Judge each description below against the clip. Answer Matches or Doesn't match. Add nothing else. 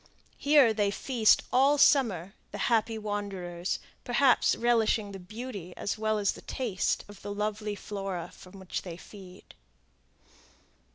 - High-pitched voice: Matches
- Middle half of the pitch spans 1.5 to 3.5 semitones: Matches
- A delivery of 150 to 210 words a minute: Doesn't match